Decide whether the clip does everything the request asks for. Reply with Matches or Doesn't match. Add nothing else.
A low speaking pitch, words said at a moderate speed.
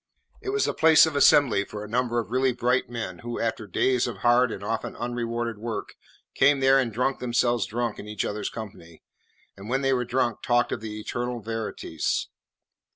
Matches